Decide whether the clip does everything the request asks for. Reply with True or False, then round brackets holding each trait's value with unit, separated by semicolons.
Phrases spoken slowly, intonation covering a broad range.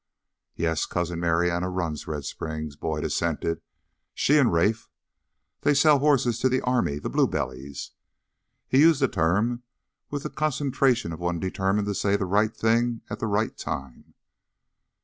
False (155 wpm; 7.1 semitones)